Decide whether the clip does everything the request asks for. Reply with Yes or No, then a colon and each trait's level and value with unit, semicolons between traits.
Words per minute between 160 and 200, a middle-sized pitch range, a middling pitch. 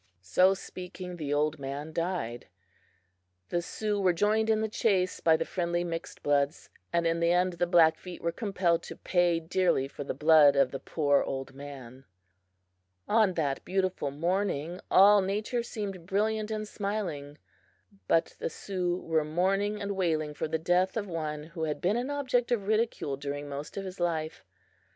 Yes: average, 170 wpm; average, 4.4 semitones; medium, 175 Hz